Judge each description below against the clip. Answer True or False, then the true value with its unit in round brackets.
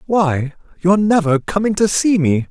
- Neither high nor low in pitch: True (180 Hz)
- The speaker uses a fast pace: False (145 wpm)